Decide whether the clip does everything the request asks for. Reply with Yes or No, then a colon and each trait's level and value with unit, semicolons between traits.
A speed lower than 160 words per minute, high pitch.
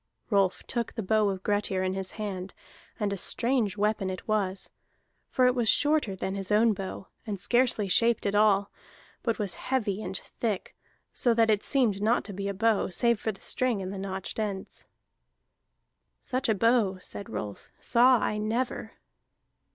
No: average, 180 wpm; high, 210 Hz